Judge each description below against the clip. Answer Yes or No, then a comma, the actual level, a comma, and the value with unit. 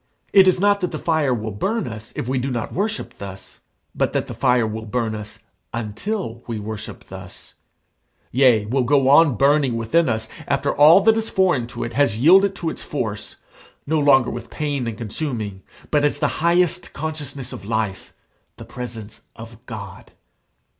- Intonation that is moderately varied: No, wide, 6.0 semitones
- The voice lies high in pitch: No, low, 130 Hz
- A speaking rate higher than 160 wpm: Yes, average, 180 wpm